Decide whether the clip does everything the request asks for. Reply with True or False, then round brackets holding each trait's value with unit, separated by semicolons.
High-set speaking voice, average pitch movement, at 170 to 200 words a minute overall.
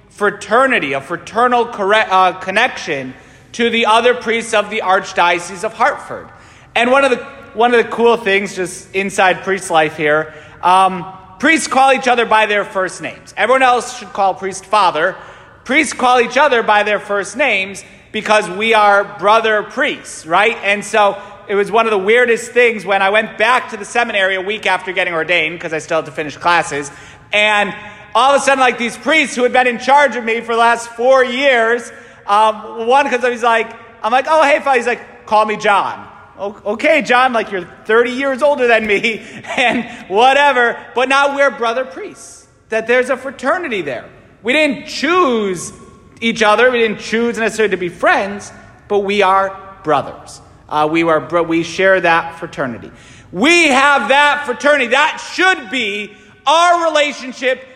True (220 Hz; 4.6 semitones; 180 wpm)